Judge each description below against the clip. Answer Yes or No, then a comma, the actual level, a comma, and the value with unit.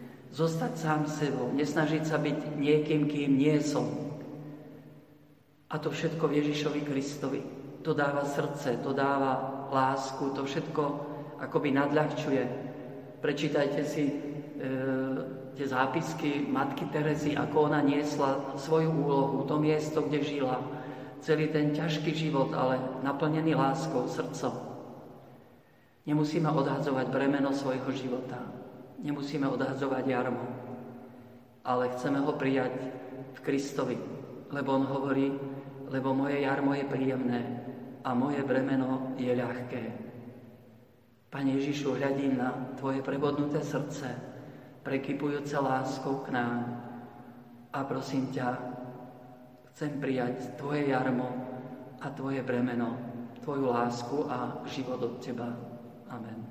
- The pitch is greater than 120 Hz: Yes, low, 135 Hz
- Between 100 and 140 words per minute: Yes, slow, 110 wpm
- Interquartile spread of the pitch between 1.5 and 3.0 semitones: Yes, narrow, 2.5 semitones